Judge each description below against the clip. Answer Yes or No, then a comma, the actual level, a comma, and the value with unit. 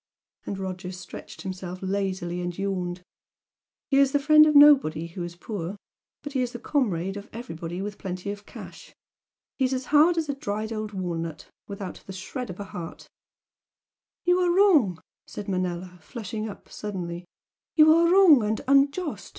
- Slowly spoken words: No, average, 165 wpm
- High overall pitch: Yes, high, 205 Hz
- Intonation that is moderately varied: No, wide, 7.3 semitones